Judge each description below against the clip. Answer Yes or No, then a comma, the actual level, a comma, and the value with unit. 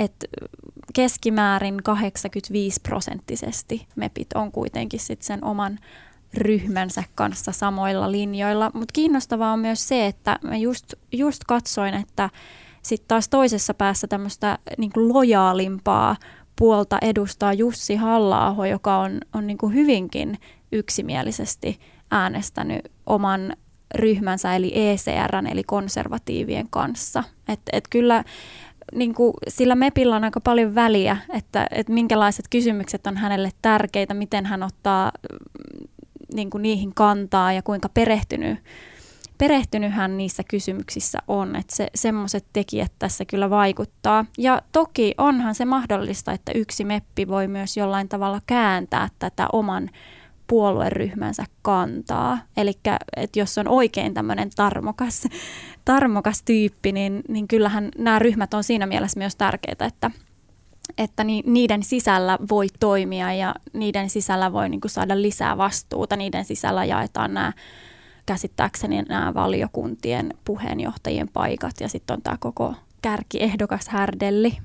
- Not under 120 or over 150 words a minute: Yes, average, 125 wpm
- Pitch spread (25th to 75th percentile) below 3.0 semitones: Yes, narrow, 2.5 semitones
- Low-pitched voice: No, high, 210 Hz